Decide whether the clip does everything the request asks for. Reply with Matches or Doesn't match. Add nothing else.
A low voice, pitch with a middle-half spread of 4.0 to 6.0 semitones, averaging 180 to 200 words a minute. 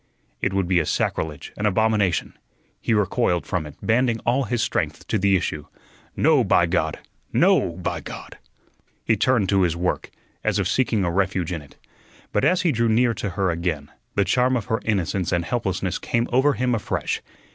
Matches